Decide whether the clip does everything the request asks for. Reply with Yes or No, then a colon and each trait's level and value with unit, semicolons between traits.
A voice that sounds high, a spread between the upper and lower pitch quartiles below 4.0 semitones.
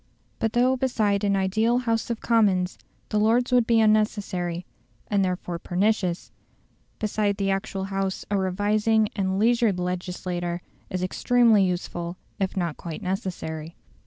Yes: high, 195 Hz; average, 3.3 semitones